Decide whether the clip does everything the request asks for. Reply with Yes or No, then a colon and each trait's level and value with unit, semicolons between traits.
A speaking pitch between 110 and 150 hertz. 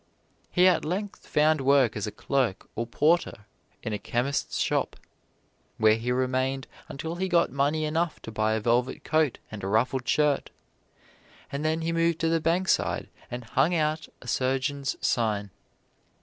Yes: medium, 140 Hz